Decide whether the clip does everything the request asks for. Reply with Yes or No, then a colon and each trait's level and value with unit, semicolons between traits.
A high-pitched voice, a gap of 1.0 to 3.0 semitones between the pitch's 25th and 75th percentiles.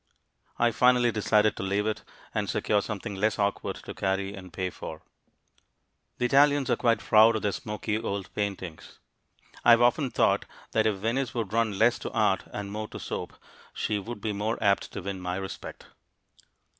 No: low, 105 Hz; average, 2.7 semitones